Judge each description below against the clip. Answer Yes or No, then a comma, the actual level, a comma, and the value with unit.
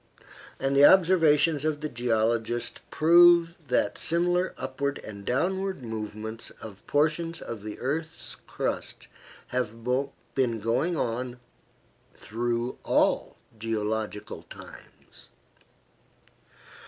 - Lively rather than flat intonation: Yes, wide, 6.2 semitones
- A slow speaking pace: Yes, slow, 95 wpm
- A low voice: Yes, low, 130 Hz